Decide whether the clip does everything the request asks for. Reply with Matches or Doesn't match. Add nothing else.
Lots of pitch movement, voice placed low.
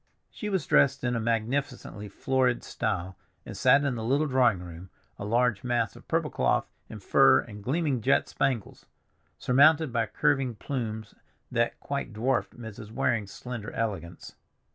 Doesn't match